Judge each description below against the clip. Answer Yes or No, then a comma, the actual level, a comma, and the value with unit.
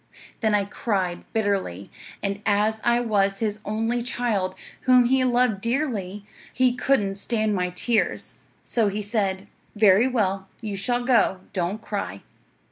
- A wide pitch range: No, average, 3.4 semitones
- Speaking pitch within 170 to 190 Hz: No, high, 210 Hz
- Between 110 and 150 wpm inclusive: Yes, average, 140 wpm